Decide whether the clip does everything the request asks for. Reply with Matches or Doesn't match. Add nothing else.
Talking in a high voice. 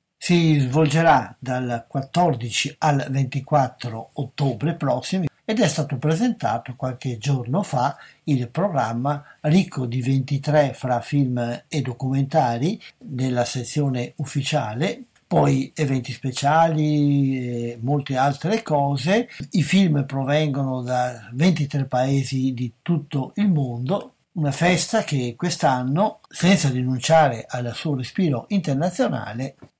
Doesn't match